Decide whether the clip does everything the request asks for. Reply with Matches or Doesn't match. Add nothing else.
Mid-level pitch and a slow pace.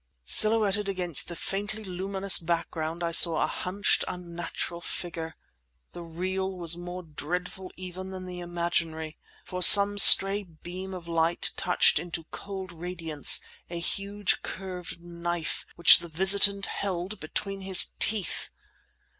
Matches